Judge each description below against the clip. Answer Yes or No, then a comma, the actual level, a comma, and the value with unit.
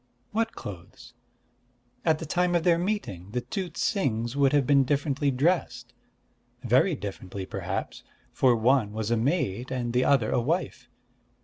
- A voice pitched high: No, low, 130 Hz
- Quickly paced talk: No, average, 150 wpm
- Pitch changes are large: Yes, wide, 6.0 semitones